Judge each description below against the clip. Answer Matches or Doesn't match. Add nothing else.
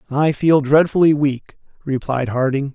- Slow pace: Matches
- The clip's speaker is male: Matches